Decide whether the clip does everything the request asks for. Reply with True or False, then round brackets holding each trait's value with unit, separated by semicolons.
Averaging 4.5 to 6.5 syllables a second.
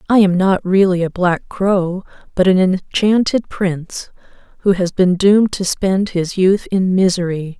False (4.3 syllables/s)